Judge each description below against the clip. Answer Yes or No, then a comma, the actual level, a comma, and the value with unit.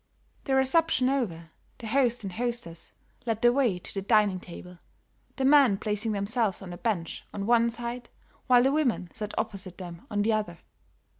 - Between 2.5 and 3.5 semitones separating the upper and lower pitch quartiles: No, average, 4.2 semitones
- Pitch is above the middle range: Yes, high, 220 Hz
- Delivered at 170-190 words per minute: Yes, average, 175 wpm